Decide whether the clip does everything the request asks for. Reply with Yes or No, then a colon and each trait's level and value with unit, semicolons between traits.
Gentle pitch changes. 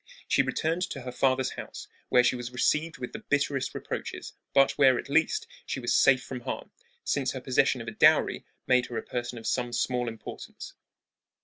Yes: narrow, 2.1 semitones